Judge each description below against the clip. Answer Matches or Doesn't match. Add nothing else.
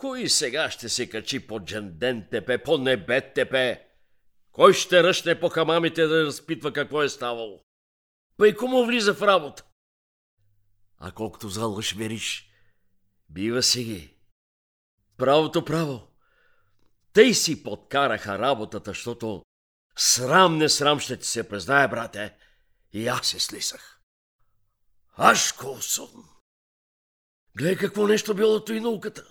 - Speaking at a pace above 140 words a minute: Doesn't match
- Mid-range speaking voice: Doesn't match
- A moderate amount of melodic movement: Doesn't match